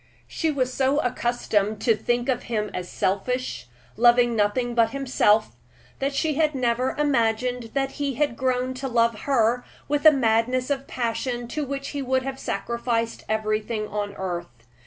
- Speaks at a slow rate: No, average, 155 wpm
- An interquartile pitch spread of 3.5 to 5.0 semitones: No, average, 3.1 semitones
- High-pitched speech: Yes, high, 245 Hz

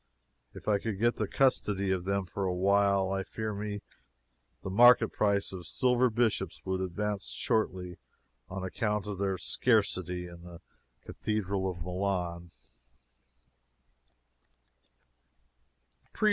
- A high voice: No, low, 100 Hz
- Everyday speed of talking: No, slow, 125 wpm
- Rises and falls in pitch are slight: Yes, narrow, 2.3 semitones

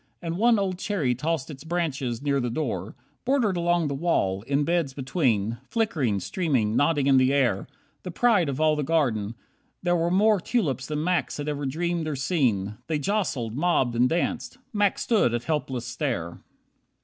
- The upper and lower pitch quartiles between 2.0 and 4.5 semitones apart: No, wide, 5.5 semitones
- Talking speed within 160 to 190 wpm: Yes, average, 175 wpm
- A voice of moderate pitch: Yes, medium, 150 Hz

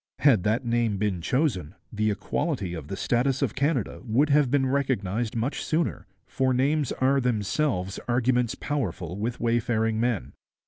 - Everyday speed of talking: Yes, average, 150 wpm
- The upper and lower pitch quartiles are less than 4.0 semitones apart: No, average, 4.3 semitones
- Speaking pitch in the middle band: No, low, 120 Hz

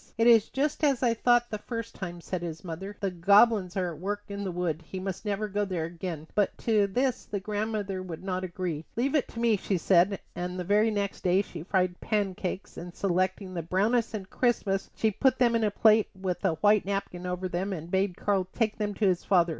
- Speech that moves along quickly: Yes, fast, 225 wpm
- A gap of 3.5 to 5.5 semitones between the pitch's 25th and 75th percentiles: No, average, 3.0 semitones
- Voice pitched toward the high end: Yes, high, 195 Hz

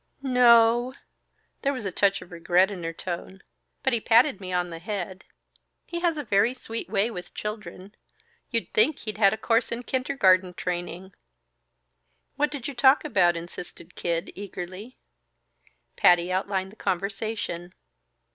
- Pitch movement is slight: No, average, 4.7 semitones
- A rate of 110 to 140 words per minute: No, average, 155 wpm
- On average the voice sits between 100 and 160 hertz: No, high, 200 Hz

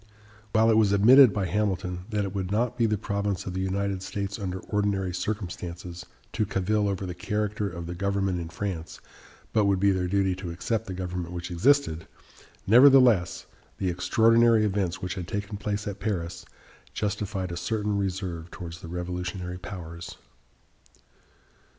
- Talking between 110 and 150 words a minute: No, average, 160 wpm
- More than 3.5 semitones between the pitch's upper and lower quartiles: No, average, 2.7 semitones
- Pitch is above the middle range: No, very low, 95 Hz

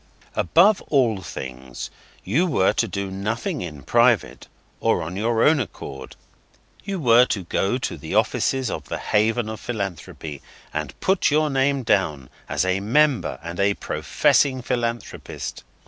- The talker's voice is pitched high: No, low, 110 Hz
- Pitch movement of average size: No, wide, 6.4 semitones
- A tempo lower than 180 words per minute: Yes, average, 145 wpm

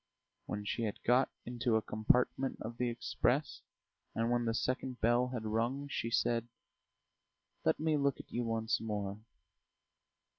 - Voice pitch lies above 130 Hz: No, low, 120 Hz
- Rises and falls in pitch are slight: Yes, narrow, 2.0 semitones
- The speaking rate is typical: Yes, average, 150 wpm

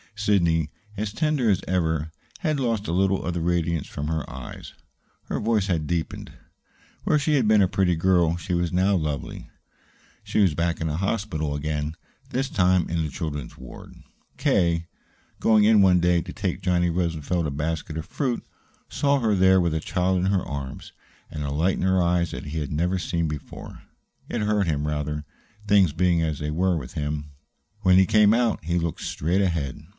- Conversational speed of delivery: Yes, average, 190 wpm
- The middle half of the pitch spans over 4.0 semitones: No, average, 3.7 semitones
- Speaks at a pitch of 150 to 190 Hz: No, very low, 85 Hz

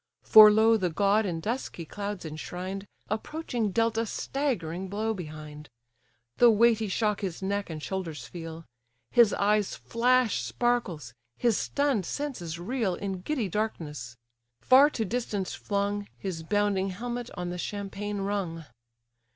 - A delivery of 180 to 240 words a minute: No, slow, 135 wpm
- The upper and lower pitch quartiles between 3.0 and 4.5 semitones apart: Yes, average, 4.2 semitones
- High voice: Yes, high, 205 Hz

